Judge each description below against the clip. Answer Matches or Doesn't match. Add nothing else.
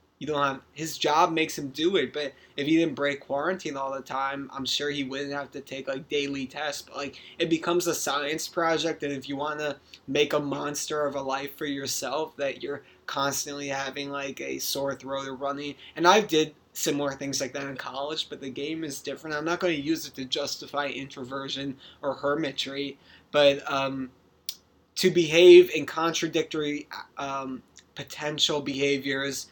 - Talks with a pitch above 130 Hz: Matches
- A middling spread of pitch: Doesn't match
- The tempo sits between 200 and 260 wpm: Doesn't match